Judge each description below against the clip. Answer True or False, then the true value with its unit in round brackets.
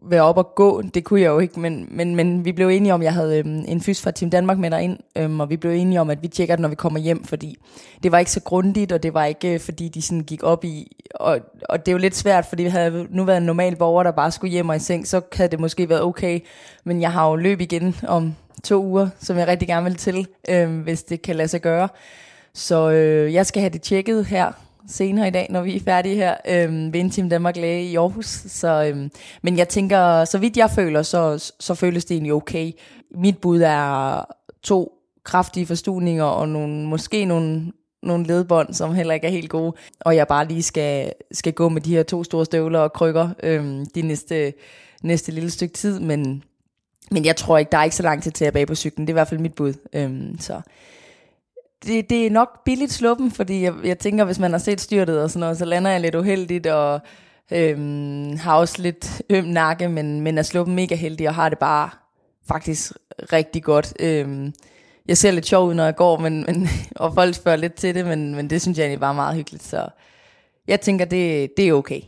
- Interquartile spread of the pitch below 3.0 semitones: True (2.4 semitones)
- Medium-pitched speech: True (170 Hz)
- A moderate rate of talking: False (235 wpm)